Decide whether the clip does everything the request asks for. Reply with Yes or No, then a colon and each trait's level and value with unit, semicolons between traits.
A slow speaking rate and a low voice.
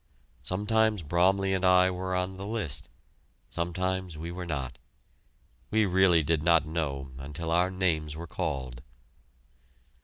Yes: slow, 130 wpm; very low, 85 Hz